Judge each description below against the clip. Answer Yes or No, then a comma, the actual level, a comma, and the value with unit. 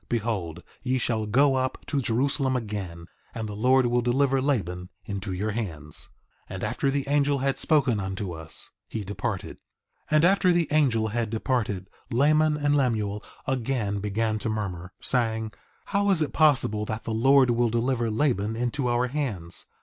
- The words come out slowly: No, average, 170 wpm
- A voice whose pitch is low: Yes, low, 120 Hz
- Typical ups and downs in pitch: Yes, average, 4.6 semitones